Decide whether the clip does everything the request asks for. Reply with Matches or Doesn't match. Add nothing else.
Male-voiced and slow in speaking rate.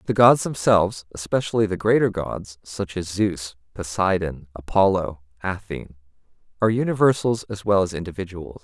Matches